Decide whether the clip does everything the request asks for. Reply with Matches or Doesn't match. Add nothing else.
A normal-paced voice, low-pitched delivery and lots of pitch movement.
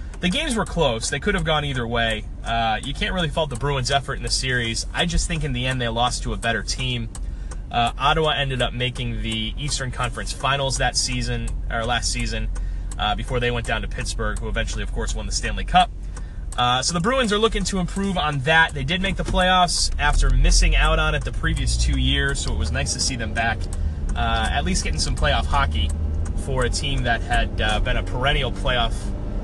Doesn't match